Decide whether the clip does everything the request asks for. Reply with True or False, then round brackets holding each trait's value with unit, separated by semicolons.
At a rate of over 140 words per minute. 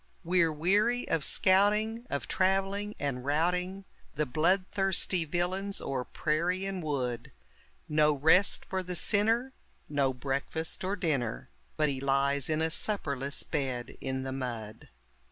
False (135 wpm)